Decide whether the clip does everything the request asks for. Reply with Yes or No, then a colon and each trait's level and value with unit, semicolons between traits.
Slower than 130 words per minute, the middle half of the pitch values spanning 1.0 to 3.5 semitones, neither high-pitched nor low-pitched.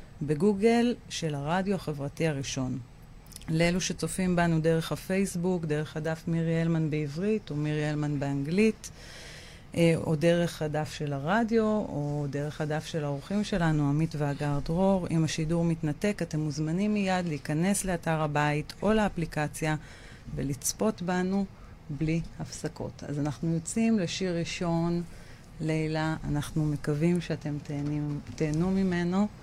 Yes: average, 120 wpm; average, 3.1 semitones; medium, 160 Hz